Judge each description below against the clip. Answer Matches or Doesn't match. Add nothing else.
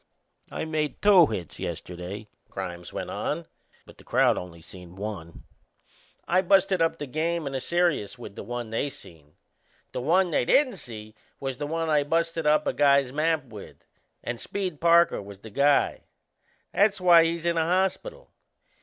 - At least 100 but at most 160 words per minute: Doesn't match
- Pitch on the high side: Doesn't match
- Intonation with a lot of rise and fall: Matches